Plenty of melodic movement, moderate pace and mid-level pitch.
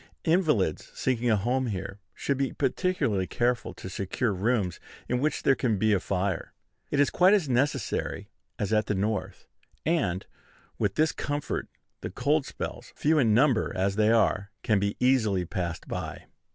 No: wide, 5.8 semitones; average, 165 wpm; low, 115 Hz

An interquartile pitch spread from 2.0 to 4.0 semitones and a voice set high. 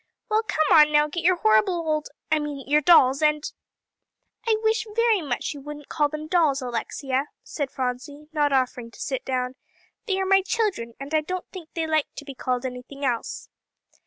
No: average, 4.5 semitones; very high, 295 Hz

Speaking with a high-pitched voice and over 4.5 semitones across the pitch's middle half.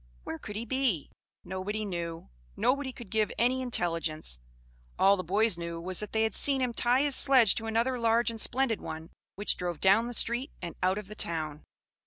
Yes: high, 215 Hz; wide, 5.4 semitones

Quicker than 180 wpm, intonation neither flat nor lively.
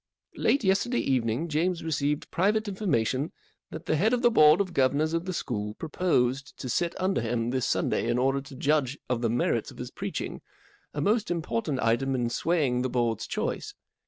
No: average, 190 wpm; wide, 5.9 semitones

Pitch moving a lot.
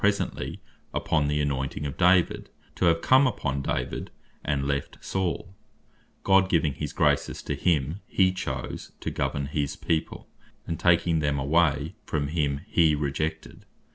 No: average, 3.6 semitones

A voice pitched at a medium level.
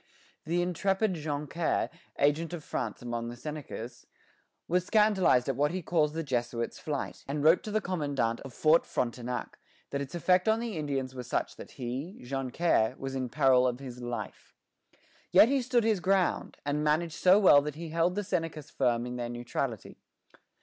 Yes: medium, 150 Hz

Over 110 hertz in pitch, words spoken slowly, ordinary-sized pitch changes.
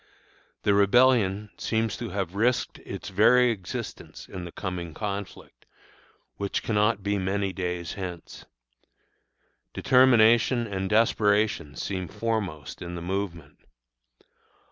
No: low, 100 Hz; slow, 110 wpm; average, 3.4 semitones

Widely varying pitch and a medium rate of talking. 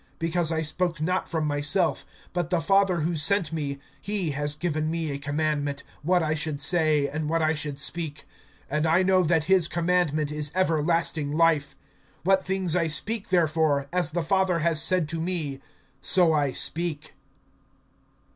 No: average, 2.8 semitones; average, 165 wpm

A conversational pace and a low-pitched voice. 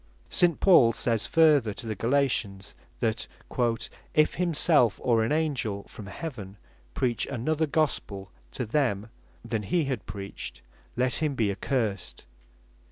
No: slow, 130 wpm; low, 120 Hz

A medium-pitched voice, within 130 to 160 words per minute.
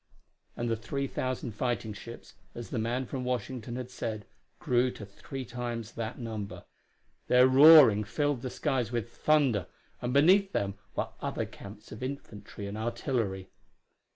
No: low, 120 Hz; average, 155 wpm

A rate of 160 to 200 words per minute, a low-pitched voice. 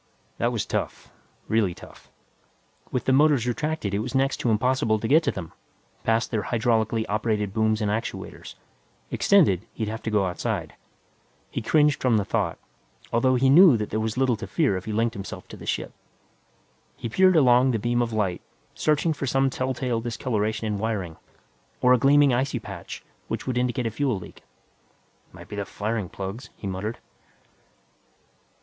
Yes: average, 175 wpm; low, 115 Hz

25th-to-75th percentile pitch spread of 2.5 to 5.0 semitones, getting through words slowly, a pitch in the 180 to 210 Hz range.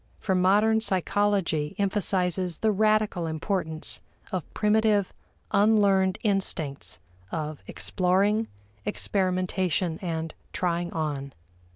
Yes: average, 3.7 semitones; slow, 85 wpm; medium, 185 Hz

